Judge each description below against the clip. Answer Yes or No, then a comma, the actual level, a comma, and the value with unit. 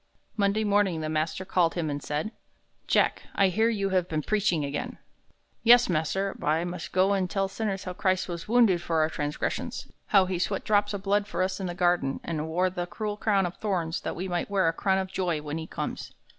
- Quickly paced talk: Yes, fast, 220 wpm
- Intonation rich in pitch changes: No, average, 3.3 semitones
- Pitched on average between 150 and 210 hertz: Yes, medium, 185 Hz